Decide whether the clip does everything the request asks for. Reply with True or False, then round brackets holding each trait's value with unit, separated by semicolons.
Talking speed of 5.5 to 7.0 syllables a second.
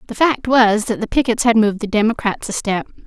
True (5.9 syllables/s)